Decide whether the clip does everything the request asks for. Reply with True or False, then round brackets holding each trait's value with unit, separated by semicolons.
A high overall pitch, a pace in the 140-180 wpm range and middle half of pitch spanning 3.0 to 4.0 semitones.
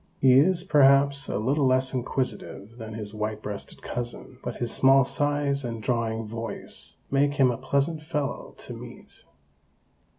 False (130 Hz; 155 wpm; 3.5 semitones)